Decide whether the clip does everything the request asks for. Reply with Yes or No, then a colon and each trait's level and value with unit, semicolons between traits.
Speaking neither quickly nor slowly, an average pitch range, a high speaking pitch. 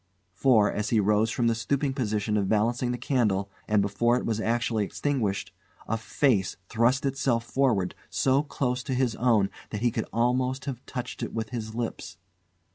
No: average, 180 wpm; average, 3.0 semitones; low, 115 Hz